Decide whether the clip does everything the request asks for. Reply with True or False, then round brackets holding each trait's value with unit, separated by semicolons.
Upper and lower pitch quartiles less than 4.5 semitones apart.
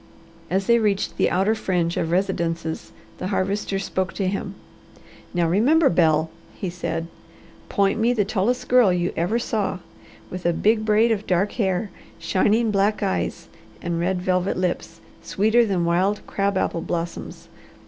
True (3.3 semitones)